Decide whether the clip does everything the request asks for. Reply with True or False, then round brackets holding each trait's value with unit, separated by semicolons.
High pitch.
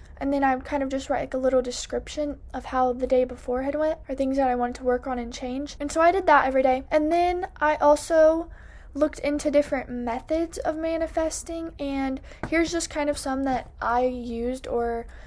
True (280 Hz)